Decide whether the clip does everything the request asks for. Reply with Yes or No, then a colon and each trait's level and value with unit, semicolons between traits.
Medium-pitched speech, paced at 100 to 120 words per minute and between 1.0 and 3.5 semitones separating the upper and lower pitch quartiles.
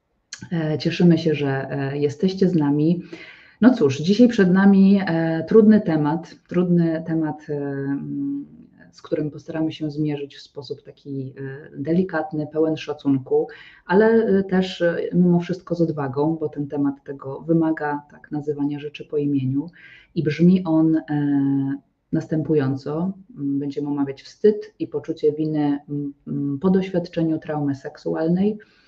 Yes: medium, 155 Hz; average, 115 wpm; average, 3.2 semitones